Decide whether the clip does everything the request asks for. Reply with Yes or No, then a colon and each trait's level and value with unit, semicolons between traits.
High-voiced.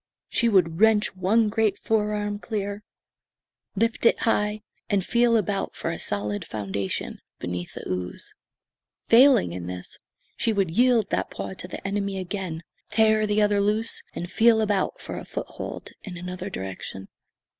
Yes: high, 200 Hz